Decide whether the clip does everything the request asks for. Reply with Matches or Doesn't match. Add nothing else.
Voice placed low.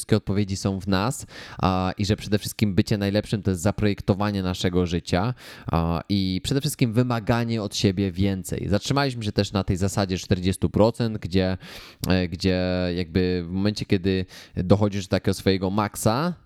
Matches